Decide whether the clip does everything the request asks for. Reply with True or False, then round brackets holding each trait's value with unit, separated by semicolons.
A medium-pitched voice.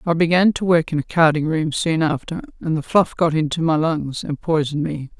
True (160 Hz)